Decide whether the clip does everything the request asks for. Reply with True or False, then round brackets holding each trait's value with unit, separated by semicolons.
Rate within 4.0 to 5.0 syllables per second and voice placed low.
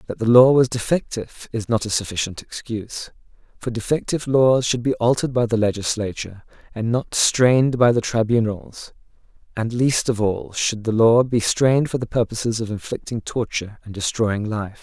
False (5.3 syllables/s; 115 Hz)